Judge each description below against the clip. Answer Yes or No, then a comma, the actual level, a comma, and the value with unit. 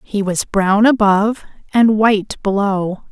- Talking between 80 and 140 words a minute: Yes, slow, 135 wpm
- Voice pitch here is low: No, high, 205 Hz